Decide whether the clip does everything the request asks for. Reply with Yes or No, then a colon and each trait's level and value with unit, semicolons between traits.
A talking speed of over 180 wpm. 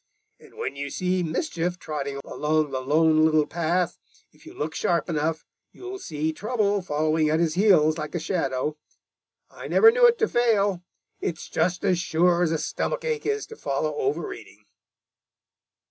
No: average, 165 wpm